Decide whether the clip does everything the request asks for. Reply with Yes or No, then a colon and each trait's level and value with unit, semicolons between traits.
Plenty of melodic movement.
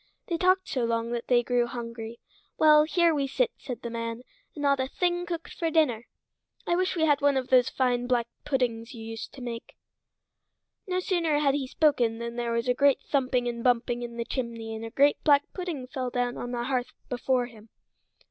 No: average, 3.7 semitones